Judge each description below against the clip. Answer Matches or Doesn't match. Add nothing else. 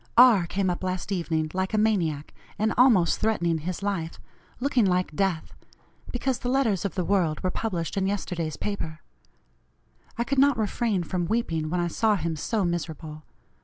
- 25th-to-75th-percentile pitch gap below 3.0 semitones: Doesn't match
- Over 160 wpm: Matches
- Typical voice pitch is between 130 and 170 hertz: Doesn't match